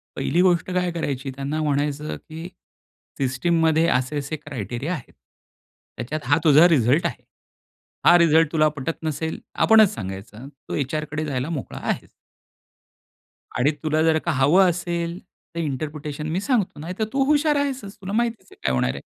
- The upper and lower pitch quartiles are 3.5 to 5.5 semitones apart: Yes, average, 3.8 semitones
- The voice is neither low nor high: Yes, medium, 155 Hz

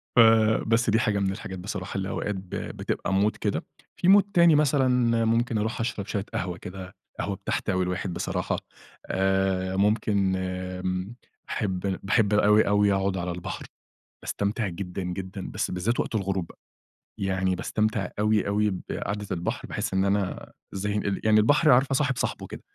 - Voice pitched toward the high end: No, low, 100 Hz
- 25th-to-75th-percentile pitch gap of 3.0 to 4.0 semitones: No, narrow, 2.6 semitones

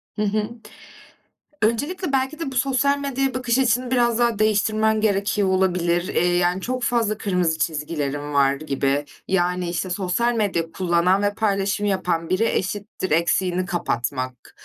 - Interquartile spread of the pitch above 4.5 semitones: Yes, average, 5.1 semitones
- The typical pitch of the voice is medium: No, high, 195 Hz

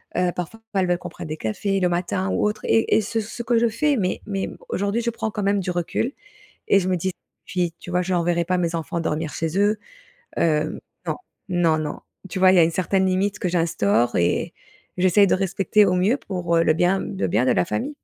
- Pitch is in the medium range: Yes, medium, 180 Hz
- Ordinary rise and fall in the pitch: Yes, average, 3.0 semitones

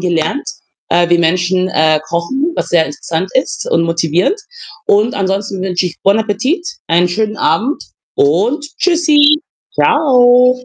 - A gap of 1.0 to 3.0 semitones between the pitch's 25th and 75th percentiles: No, wide, 6.9 semitones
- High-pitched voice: Yes, high, 195 Hz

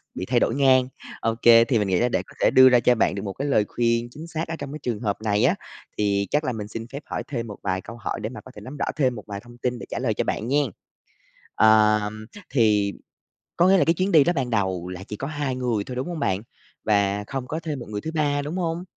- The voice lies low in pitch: Yes, low, 120 Hz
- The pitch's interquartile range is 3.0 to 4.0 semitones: No, average, 5.2 semitones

